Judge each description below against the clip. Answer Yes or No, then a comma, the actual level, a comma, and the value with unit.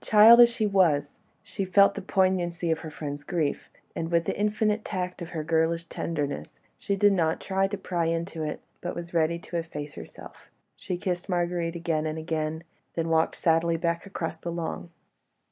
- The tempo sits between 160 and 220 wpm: Yes, average, 185 wpm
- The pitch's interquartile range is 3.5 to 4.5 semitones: No, narrow, 2.6 semitones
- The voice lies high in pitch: No, medium, 170 Hz